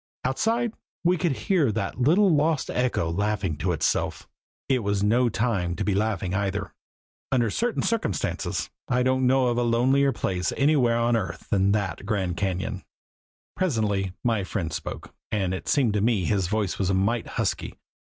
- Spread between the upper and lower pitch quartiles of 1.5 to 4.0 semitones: No, average, 5.1 semitones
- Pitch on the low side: Yes, low, 110 Hz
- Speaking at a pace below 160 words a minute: No, average, 170 wpm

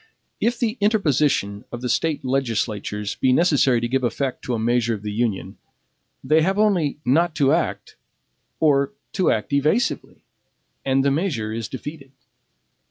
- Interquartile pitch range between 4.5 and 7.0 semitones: Yes, average, 5.3 semitones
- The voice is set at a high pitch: No, low, 135 Hz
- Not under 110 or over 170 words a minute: Yes, average, 155 wpm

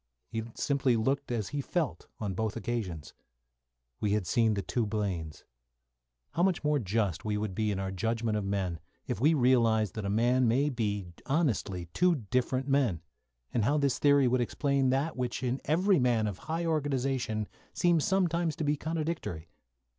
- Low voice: Yes, low, 120 Hz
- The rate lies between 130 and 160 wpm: No, average, 175 wpm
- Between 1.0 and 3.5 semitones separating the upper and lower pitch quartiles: No, wide, 5.4 semitones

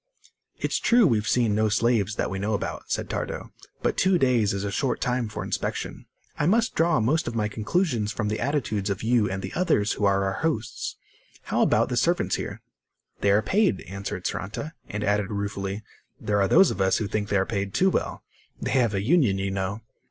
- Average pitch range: Yes, average, 4.1 semitones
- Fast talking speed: Yes, fast, 210 wpm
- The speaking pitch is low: Yes, low, 105 Hz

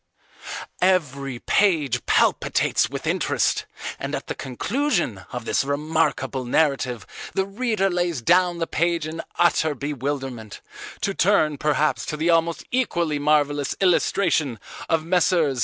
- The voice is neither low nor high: Yes, medium, 155 Hz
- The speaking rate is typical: No, slow, 125 wpm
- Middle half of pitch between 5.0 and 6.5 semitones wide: No, average, 4.2 semitones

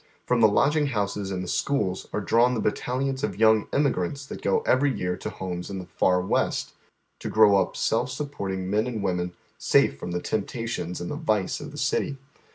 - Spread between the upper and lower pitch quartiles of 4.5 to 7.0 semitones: Yes, wide, 5.4 semitones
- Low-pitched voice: Yes, low, 105 Hz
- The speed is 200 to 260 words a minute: Yes, fast, 205 wpm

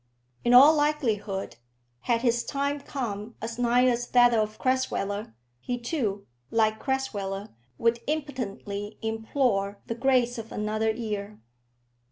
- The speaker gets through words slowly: Yes, slow, 125 wpm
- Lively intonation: No, average, 3.5 semitones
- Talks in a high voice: Yes, high, 230 Hz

